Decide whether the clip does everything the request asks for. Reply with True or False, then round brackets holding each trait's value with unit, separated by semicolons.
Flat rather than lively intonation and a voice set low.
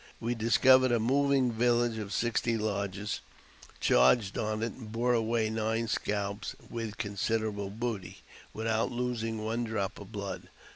True (1.8 semitones; 115 Hz)